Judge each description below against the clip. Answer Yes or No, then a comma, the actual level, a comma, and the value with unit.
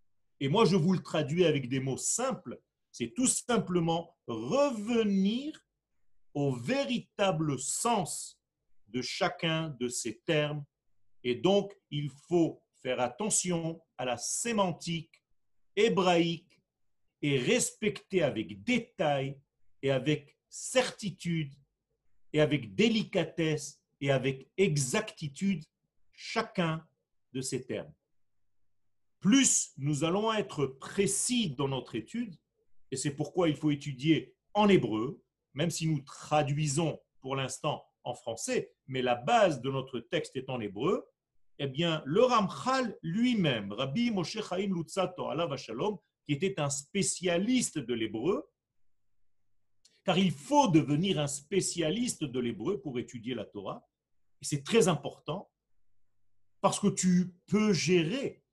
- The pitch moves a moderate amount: No, wide, 6.5 semitones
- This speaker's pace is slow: Yes, slow, 125 wpm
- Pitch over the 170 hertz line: No, medium, 155 Hz